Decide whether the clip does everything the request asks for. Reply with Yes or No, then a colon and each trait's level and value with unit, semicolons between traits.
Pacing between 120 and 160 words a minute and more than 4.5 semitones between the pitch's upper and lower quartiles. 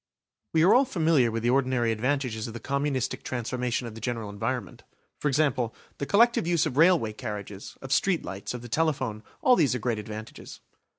No: average, 190 wpm; average, 4.9 semitones